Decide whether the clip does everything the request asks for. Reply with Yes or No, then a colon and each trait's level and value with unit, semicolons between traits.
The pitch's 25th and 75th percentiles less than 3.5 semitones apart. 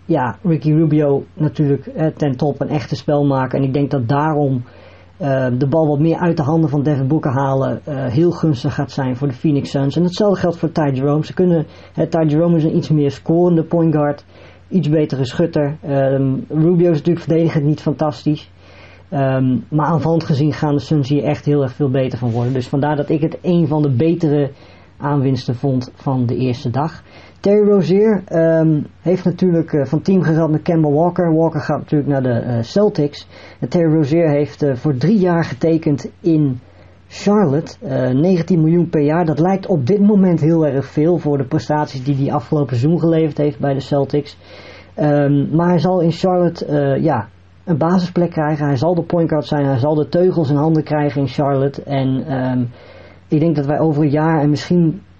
Yes: average, 3.0 semitones